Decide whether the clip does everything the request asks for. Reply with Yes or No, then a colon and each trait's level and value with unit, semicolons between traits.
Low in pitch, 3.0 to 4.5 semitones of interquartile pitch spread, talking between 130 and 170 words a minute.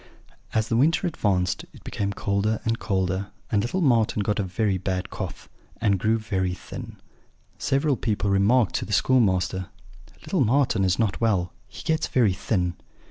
Yes: low, 105 Hz; average, 3.7 semitones; average, 165 wpm